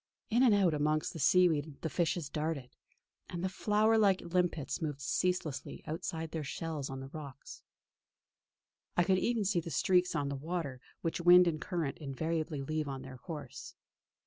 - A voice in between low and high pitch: Yes, medium, 160 Hz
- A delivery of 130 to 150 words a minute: No, average, 170 wpm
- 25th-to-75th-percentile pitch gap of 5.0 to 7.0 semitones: No, average, 3.8 semitones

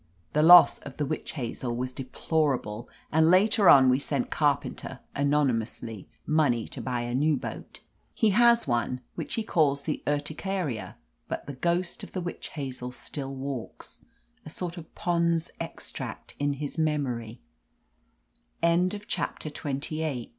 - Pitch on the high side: No, medium, 145 Hz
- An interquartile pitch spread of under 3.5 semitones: No, average, 4.3 semitones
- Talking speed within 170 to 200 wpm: No, average, 140 wpm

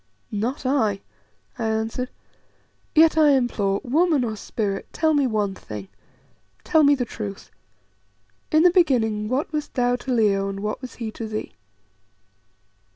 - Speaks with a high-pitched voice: Yes, high, 240 Hz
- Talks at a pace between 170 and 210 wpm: No, average, 150 wpm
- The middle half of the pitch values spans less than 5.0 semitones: No, average, 5.3 semitones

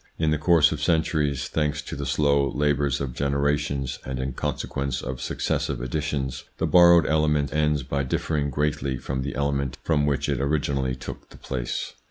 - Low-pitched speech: Yes, very low, 70 Hz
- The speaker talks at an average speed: Yes, average, 175 wpm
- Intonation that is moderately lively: No, narrow, 1.9 semitones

